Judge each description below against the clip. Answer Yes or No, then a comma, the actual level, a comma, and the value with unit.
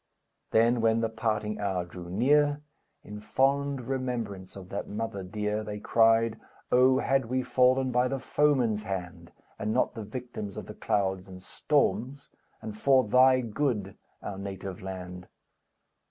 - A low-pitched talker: Yes, low, 110 Hz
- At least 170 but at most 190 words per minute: No, average, 150 wpm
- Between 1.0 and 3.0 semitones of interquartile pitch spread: No, average, 4.5 semitones